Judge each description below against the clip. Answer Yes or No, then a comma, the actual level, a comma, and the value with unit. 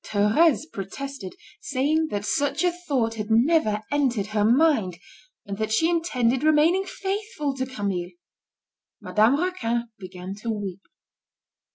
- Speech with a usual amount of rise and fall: No, wide, 6.9 semitones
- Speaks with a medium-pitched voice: No, very high, 250 Hz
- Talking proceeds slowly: Yes, slow, 130 wpm